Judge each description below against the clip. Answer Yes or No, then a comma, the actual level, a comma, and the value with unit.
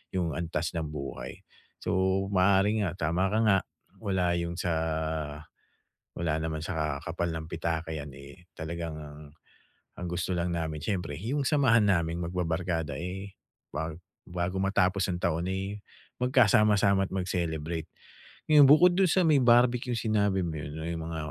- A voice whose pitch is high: No, very low, 90 Hz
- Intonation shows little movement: No, average, 3.8 semitones